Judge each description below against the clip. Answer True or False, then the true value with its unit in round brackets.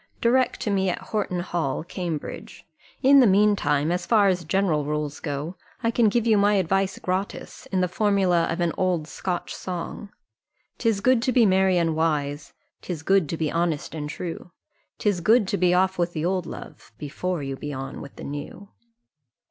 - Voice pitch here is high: False (180 Hz)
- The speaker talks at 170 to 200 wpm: True (190 wpm)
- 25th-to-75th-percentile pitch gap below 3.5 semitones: False (3.9 semitones)